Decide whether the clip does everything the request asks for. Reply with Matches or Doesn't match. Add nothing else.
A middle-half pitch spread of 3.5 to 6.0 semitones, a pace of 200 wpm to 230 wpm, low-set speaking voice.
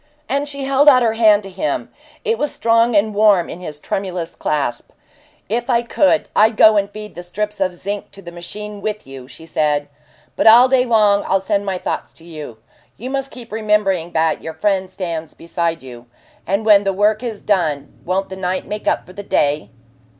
Doesn't match